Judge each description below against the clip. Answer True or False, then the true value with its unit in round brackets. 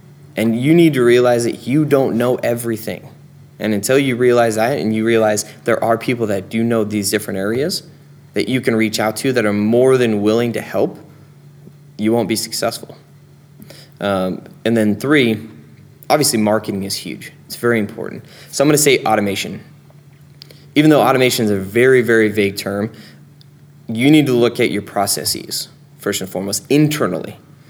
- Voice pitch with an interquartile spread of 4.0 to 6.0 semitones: True (4.9 semitones)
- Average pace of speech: True (175 wpm)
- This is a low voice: True (120 Hz)